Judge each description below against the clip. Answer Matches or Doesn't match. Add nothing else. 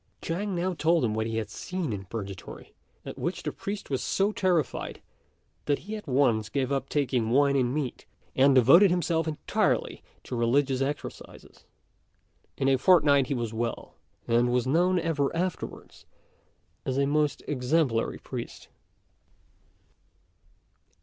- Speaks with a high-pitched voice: Doesn't match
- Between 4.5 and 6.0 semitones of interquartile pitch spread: Matches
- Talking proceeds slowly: Doesn't match